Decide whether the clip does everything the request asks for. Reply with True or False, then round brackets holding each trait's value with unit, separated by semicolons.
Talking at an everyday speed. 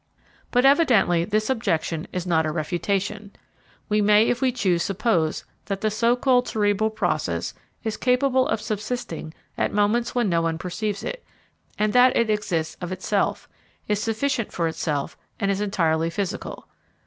True (160 wpm)